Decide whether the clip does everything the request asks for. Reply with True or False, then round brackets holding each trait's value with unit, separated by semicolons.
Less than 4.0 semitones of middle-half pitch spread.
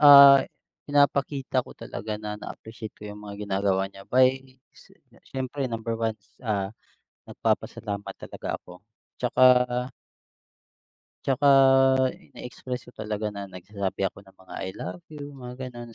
False (4.6 semitones)